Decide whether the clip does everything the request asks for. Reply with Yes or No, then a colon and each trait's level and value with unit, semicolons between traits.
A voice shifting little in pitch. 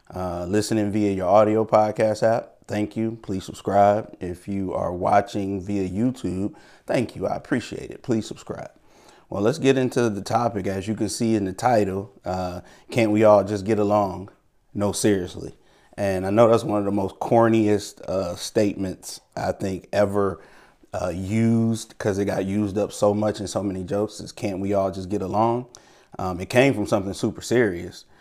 Yes: narrow, 2.2 semitones